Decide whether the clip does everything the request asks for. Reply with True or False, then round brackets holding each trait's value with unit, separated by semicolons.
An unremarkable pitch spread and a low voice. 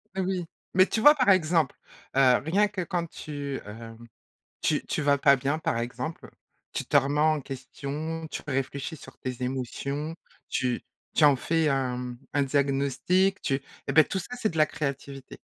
False (3.5 semitones; 145 Hz)